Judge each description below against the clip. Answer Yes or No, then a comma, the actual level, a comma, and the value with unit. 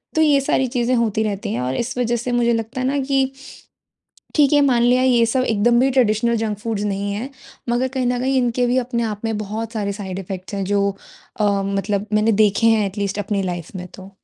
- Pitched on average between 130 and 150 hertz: No, high, 225 Hz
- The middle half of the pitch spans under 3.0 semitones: No, average, 3.6 semitones